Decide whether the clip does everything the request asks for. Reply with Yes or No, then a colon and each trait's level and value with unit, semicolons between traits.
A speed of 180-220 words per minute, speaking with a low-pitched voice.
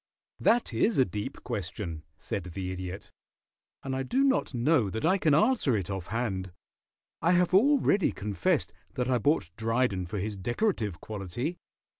No: average, 160 wpm; low, 115 Hz